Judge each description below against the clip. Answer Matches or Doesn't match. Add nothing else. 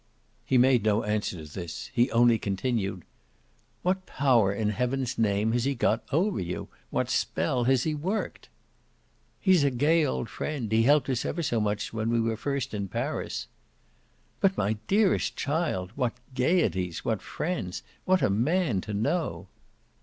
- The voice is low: Matches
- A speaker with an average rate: Matches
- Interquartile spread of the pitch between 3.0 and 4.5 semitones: Doesn't match